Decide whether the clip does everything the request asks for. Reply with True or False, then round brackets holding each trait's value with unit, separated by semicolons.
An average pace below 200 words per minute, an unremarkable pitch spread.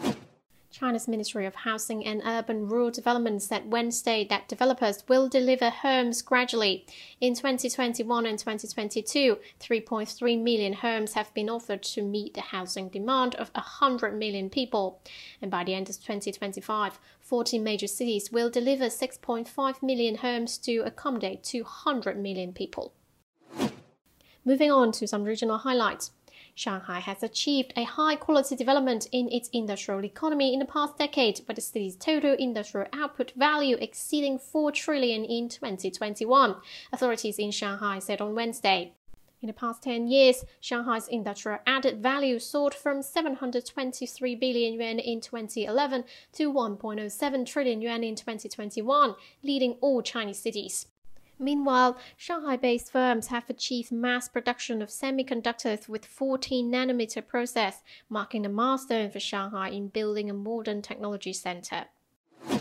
True (140 wpm; 3.4 semitones)